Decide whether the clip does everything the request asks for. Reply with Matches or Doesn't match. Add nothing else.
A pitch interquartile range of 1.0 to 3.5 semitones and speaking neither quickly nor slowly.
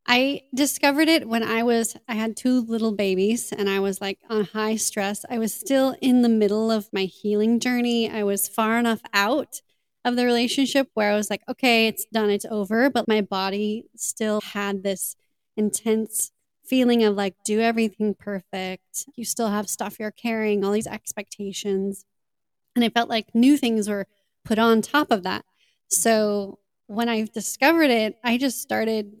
Matches